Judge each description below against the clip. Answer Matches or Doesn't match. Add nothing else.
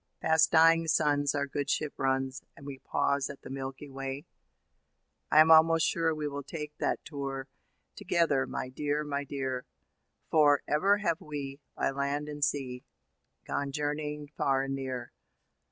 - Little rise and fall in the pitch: Matches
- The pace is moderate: Matches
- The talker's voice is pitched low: Doesn't match